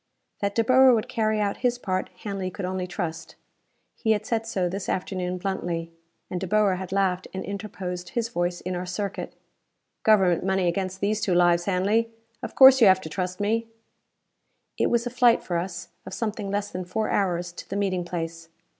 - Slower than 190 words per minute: No, average, 195 wpm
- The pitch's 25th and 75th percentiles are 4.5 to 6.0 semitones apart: No, average, 3.0 semitones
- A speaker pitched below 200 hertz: Yes, high, 190 Hz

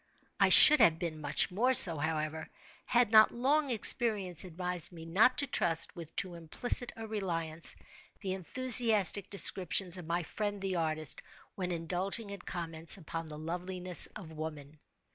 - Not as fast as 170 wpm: Yes, average, 155 wpm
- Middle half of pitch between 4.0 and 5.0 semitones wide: Yes, average, 4.3 semitones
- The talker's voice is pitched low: No, medium, 180 Hz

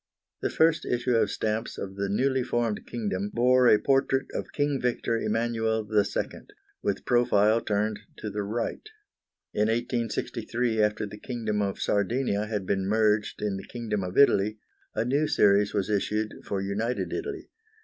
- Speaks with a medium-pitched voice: No, low, 110 Hz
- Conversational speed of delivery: Yes, average, 160 wpm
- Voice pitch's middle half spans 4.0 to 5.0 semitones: No, average, 2.8 semitones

